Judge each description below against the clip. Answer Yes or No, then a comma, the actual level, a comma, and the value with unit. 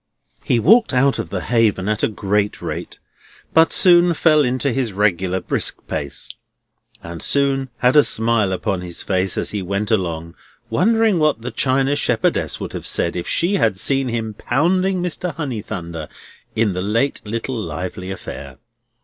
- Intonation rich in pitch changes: Yes, wide, 6.9 semitones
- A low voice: Yes, low, 115 Hz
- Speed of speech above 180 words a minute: No, average, 165 wpm